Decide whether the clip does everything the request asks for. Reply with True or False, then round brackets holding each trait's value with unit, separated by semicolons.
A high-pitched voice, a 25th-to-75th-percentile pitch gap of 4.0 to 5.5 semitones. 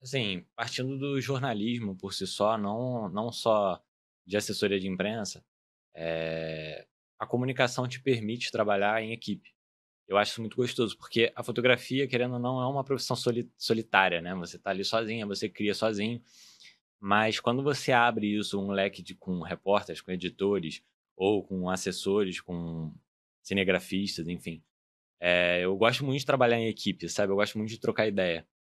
False (105 Hz; 4.6 semitones)